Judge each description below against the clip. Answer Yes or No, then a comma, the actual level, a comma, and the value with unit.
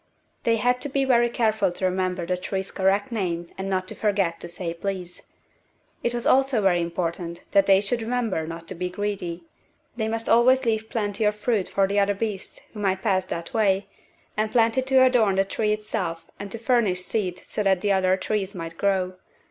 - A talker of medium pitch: No, high, 200 Hz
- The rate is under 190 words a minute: No, average, 200 wpm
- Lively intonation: No, average, 3.4 semitones